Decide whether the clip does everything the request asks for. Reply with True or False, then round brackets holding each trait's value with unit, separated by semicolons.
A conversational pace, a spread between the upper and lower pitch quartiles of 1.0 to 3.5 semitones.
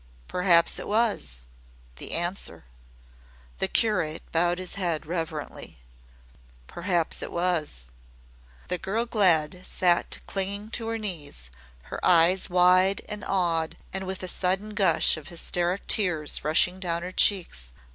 False (130 wpm; 2.7 semitones)